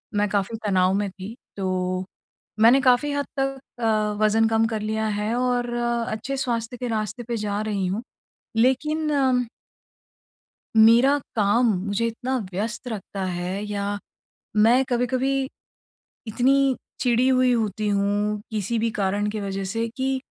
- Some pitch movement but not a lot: Yes, average, 3.3 semitones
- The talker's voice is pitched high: Yes, high, 225 Hz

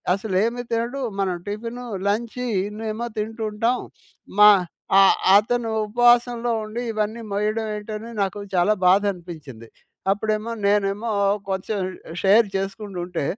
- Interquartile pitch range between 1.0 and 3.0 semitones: Yes, narrow, 2.6 semitones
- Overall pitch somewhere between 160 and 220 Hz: Yes, high, 210 Hz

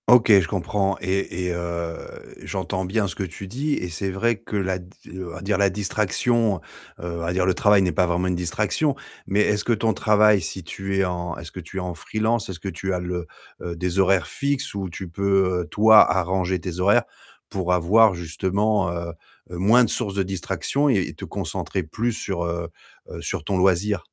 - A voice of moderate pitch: No, very low, 95 Hz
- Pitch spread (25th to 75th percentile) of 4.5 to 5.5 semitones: No, average, 2.8 semitones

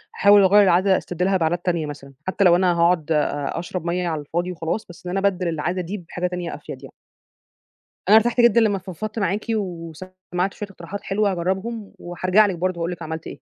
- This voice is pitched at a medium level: Yes, medium, 180 Hz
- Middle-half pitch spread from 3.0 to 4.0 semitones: No, narrow, 2.6 semitones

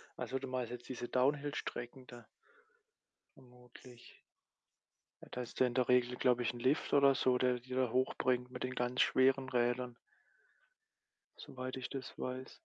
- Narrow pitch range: Yes, narrow, 1.0 semitones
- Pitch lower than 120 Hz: No, low, 125 Hz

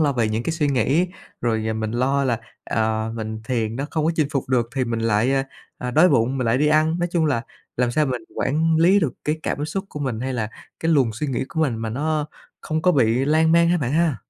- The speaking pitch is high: No, low, 135 Hz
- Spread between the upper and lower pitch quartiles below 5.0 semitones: No, average, 5.3 semitones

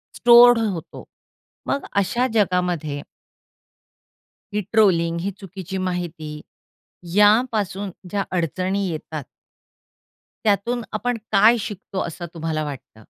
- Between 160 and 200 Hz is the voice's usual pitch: Yes, high, 190 Hz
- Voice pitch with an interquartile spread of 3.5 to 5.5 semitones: Yes, average, 4.1 semitones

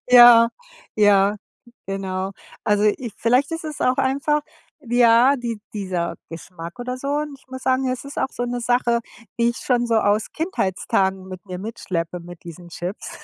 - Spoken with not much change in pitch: No, average, 5.0 semitones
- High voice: Yes, high, 230 Hz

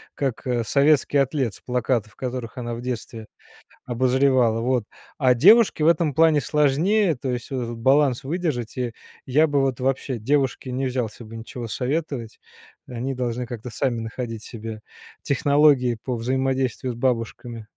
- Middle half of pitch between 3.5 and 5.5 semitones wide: No, average, 2.9 semitones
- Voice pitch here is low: Yes, low, 125 Hz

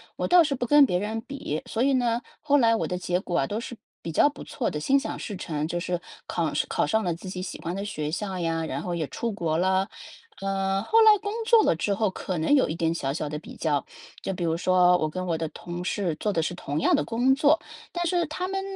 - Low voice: No, medium, 185 Hz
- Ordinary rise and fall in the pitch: No, wide, 6.7 semitones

